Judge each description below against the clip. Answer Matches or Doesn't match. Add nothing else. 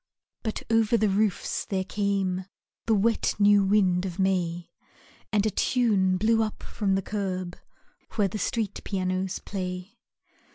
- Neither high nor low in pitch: Doesn't match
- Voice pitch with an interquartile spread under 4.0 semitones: Matches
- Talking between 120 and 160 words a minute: Matches